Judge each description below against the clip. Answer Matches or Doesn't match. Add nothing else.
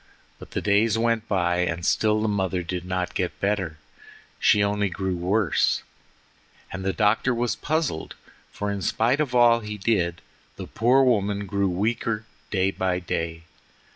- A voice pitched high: Doesn't match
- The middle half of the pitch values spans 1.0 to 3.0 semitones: Doesn't match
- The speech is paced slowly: Doesn't match